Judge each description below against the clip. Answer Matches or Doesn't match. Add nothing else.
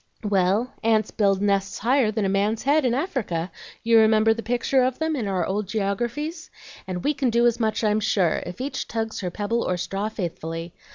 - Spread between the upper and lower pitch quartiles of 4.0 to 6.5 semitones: Doesn't match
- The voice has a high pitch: Matches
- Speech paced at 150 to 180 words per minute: Doesn't match